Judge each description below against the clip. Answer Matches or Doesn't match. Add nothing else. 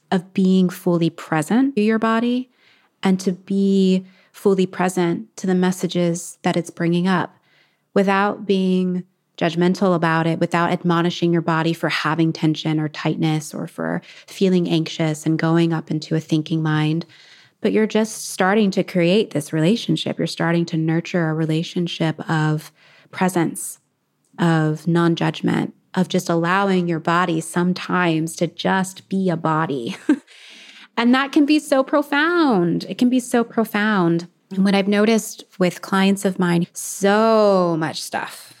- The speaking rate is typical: Matches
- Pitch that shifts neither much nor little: Matches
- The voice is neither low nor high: Matches